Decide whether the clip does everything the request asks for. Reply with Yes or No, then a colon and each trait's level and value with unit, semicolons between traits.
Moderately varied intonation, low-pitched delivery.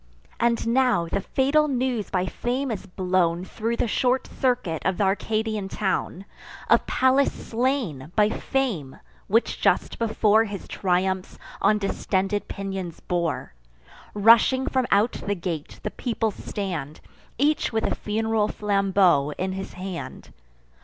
No: average, 4.0 semitones; high, 205 Hz